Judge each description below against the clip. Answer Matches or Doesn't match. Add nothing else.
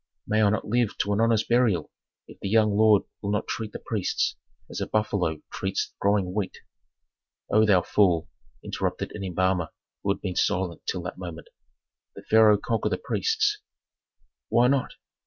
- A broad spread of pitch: Doesn't match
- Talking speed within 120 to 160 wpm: Doesn't match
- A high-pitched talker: Doesn't match